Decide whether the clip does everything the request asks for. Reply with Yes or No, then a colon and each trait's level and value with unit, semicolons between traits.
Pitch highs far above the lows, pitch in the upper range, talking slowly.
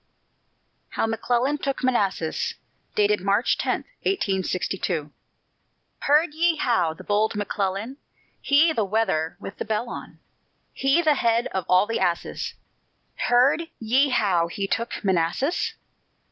Yes: wide, 6.0 semitones; high, 225 Hz; slow, 120 wpm